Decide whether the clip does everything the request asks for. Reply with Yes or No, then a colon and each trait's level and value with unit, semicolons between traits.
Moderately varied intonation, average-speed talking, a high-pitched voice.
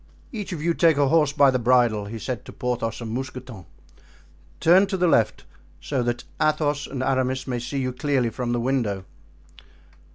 No: average, 3.5 semitones; average, 185 wpm; low, 130 Hz